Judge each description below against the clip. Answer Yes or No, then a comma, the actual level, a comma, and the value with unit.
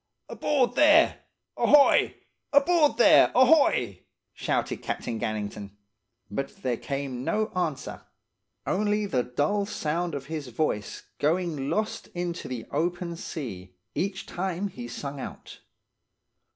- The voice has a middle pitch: Yes, medium, 165 Hz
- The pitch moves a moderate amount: No, wide, 8.4 semitones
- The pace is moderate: No, slow, 110 wpm